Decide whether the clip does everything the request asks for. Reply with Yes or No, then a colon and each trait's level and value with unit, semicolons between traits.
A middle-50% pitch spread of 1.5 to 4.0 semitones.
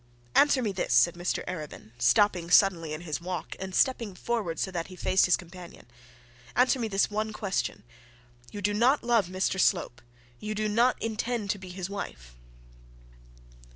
Yes: average, 3.7 semitones